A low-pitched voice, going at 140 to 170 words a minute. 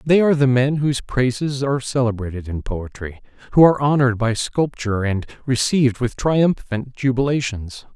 Yes: low, 125 Hz; average, 150 wpm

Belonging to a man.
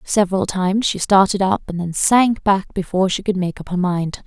No: female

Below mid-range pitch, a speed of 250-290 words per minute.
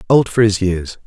No: low, 105 Hz; fast, 225 wpm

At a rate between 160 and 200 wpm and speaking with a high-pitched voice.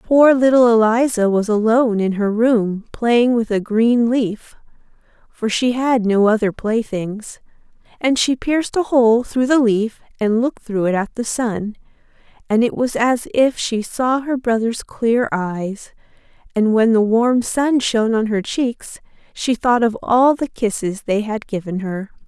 Yes: average, 170 wpm; high, 230 Hz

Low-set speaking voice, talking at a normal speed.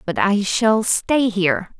No: high, 200 Hz; average, 165 wpm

